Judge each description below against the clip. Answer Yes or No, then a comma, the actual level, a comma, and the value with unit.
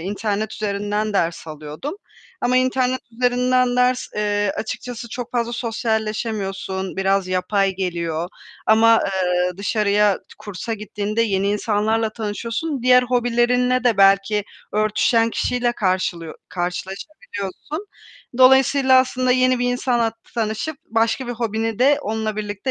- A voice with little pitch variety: No, average, 3.7 semitones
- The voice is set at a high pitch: Yes, high, 220 Hz